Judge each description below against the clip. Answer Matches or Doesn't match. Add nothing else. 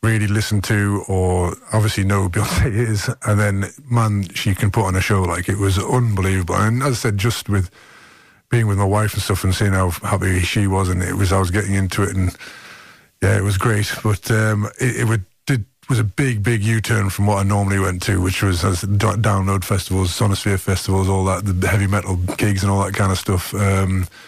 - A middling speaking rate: Doesn't match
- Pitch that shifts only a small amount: Matches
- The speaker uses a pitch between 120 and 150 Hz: Doesn't match